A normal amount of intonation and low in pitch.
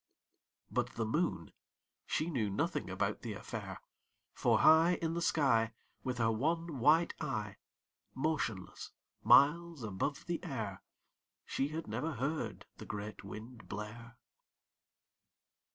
No: wide, 6.5 semitones; low, 130 Hz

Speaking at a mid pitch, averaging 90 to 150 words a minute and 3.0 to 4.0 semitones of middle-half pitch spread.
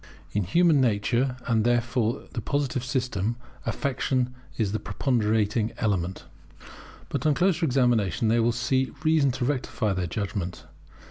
No: low, 120 Hz; average, 140 wpm; average, 3.6 semitones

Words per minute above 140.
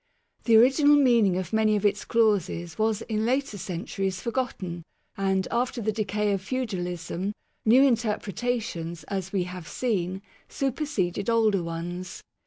No: slow, 135 wpm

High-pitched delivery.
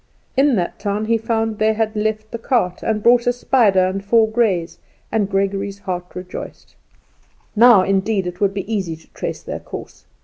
Yes: high, 210 Hz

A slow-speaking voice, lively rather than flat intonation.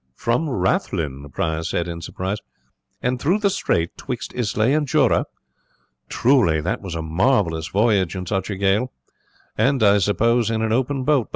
No: average, 175 wpm; wide, 6.4 semitones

